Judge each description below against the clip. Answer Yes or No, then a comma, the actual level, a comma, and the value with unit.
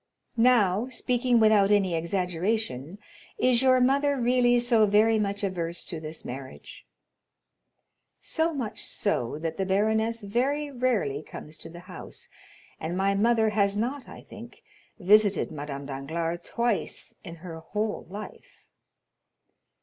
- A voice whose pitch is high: Yes, high, 205 Hz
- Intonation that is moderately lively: No, wide, 5.8 semitones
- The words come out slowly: Yes, slow, 130 wpm